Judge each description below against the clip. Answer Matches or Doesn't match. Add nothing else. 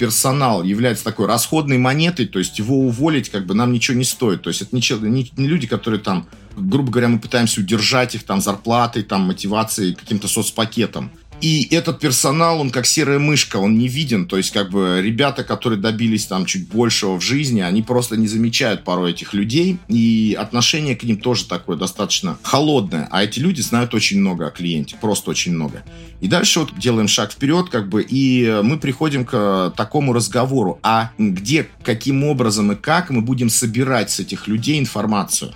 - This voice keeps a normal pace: Doesn't match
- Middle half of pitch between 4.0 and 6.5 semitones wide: Matches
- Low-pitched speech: Matches